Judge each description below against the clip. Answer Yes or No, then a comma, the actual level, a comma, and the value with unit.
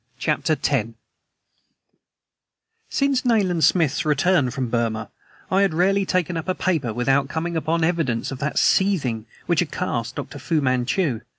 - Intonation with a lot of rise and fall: Yes, wide, 6.1 semitones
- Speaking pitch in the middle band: Yes, medium, 155 Hz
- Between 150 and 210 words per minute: Yes, average, 155 wpm